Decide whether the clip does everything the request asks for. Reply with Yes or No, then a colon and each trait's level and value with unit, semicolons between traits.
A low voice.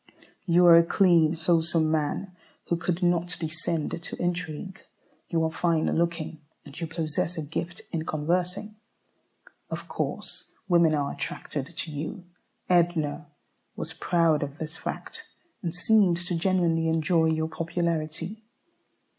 No: medium, 165 Hz